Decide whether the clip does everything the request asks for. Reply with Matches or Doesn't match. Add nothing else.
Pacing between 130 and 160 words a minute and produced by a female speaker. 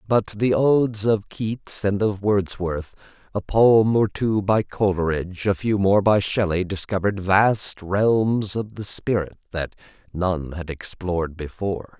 Doesn't match